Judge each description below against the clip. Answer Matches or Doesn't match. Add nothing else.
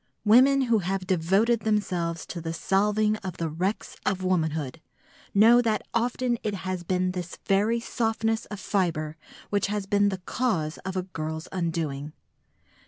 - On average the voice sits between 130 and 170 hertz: Doesn't match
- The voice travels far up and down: Doesn't match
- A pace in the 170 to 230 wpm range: Doesn't match